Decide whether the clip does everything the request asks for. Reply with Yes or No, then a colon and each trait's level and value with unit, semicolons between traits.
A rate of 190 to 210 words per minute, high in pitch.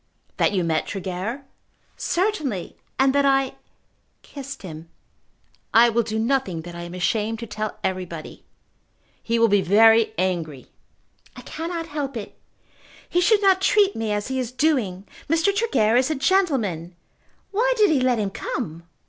No: average, 155 wpm; high, 230 Hz